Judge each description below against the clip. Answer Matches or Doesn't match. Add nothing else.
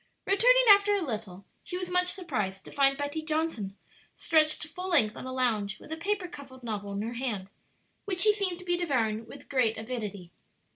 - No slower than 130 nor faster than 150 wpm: Doesn't match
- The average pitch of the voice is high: Matches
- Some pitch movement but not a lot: Doesn't match